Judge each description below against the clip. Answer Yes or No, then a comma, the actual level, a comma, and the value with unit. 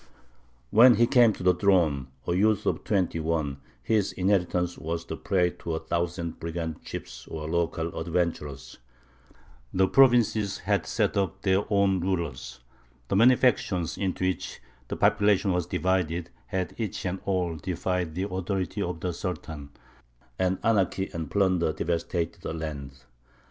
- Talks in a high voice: No, very low, 90 Hz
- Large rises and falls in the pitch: No, average, 3.0 semitones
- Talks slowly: No, average, 150 wpm